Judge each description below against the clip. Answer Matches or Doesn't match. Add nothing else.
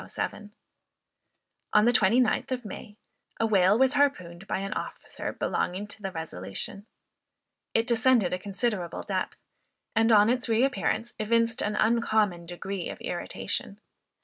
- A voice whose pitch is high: Matches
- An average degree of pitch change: Matches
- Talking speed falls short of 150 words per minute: Matches